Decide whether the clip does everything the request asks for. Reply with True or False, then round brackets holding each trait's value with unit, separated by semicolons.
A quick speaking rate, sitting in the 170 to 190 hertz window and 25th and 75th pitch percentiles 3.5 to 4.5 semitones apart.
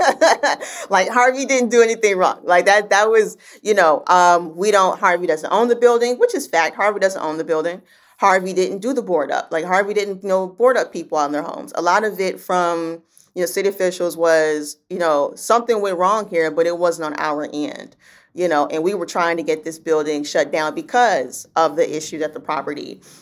True (220 wpm; 185 Hz; 4.2 semitones)